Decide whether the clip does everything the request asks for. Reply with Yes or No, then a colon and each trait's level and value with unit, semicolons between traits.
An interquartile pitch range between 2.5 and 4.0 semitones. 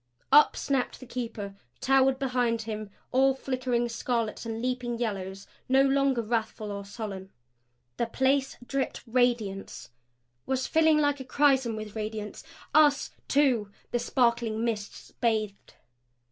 Yes: average, 3.4 semitones